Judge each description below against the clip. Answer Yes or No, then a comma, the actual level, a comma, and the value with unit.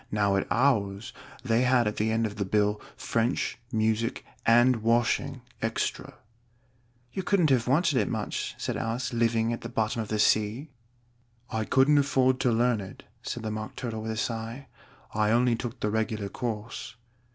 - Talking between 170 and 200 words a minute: Yes, average, 175 wpm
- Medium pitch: No, low, 115 Hz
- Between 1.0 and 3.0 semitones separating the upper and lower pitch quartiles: Yes, narrow, 2.5 semitones